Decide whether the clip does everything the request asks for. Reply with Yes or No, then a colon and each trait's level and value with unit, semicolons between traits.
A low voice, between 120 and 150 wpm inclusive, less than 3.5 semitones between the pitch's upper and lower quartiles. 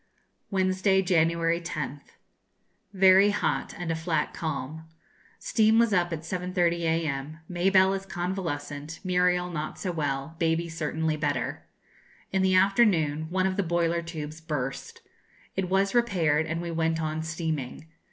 No: medium, 170 Hz; average, 140 wpm; average, 3.0 semitones